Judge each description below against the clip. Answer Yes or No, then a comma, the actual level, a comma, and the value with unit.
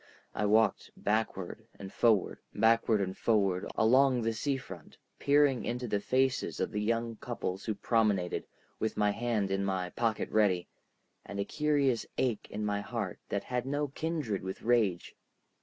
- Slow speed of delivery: No, average, 160 wpm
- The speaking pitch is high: No, low, 110 Hz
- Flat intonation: No, average, 3.6 semitones